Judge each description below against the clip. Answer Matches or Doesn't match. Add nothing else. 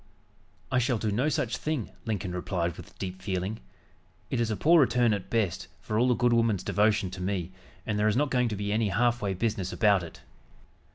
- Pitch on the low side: Matches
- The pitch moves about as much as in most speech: Matches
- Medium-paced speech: Doesn't match